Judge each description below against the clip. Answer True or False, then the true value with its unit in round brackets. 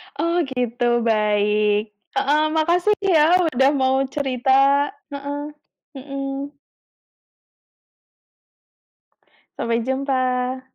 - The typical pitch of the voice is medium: False (265 Hz)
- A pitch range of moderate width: True (3.3 semitones)